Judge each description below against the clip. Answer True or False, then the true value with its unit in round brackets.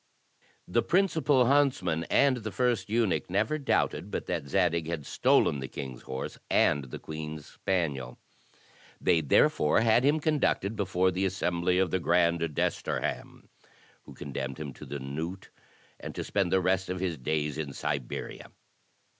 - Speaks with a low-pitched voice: True (90 Hz)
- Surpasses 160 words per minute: False (155 wpm)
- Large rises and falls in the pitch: True (6.2 semitones)